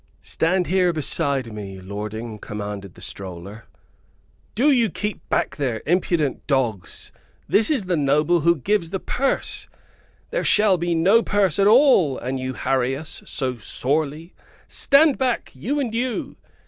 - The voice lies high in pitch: No, medium, 160 Hz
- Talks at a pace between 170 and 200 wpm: No, average, 150 wpm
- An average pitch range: No, wide, 8.6 semitones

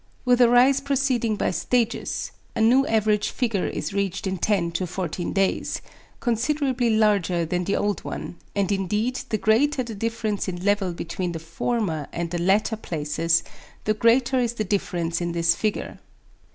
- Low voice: No, high, 205 Hz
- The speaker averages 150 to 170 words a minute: Yes, average, 165 wpm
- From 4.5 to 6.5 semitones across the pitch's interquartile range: Yes, average, 4.9 semitones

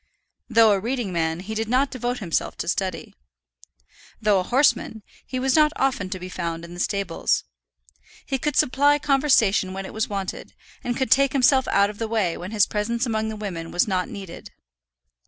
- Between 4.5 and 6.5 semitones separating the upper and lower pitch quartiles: Yes, wide, 5.4 semitones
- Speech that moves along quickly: No, average, 190 wpm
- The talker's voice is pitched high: Yes, high, 215 Hz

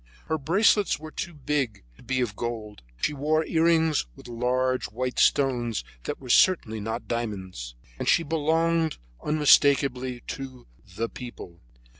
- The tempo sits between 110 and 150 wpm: Yes, average, 140 wpm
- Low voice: Yes, low, 130 Hz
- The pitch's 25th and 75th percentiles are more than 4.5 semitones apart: Yes, average, 4.9 semitones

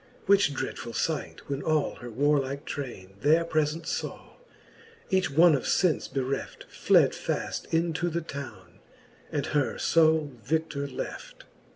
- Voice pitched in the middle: Yes, medium, 150 Hz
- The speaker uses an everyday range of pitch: Yes, average, 3.0 semitones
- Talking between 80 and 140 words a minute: Yes, slow, 135 wpm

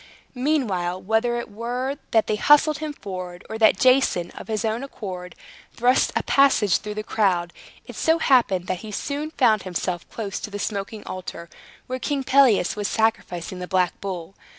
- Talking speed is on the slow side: No, average, 175 wpm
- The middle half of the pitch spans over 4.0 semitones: Yes, wide, 5.5 semitones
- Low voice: No, high, 215 Hz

